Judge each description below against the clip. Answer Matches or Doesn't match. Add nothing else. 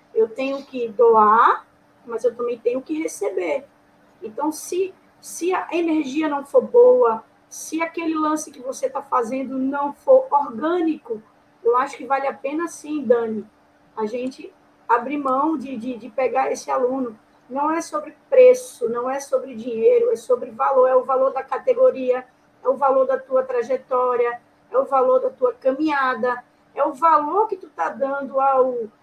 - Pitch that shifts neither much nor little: Matches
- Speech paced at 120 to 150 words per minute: Doesn't match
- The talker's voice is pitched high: Matches